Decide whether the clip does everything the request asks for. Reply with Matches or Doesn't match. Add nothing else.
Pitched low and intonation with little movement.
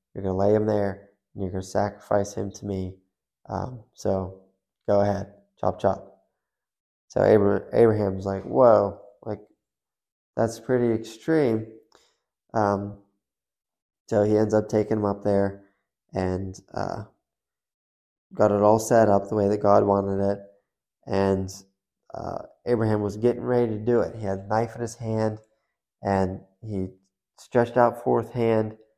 Matches